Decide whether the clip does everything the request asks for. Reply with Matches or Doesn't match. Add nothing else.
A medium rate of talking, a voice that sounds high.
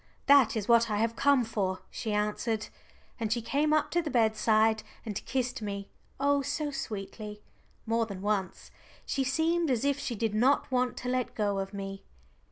Matches